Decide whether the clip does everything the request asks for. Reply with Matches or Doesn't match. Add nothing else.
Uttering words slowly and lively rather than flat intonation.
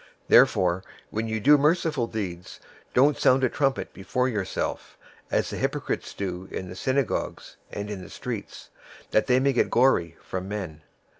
Doesn't match